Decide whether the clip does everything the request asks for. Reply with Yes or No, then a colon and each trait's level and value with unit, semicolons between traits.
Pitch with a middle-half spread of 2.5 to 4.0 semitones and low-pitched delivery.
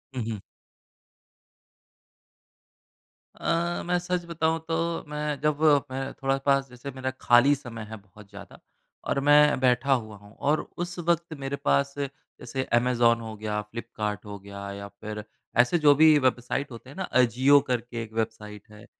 No: average, 5.0 semitones; low, 130 Hz